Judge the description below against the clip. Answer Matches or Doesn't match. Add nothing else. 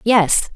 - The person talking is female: Matches